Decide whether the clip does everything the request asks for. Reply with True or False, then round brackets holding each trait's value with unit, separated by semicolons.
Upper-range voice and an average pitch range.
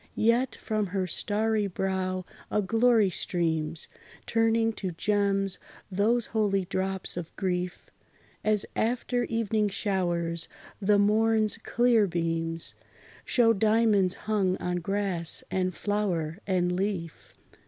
True (195 Hz; 3.3 semitones)